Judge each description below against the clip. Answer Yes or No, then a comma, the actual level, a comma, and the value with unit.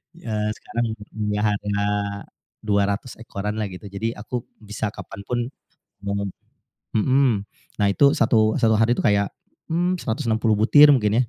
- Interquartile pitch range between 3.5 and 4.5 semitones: No, narrow, 2.4 semitones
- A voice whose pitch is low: Yes, low, 110 Hz